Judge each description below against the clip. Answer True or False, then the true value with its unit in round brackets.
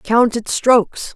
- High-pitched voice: True (235 Hz)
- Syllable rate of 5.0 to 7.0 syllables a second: False (3.6 syllables/s)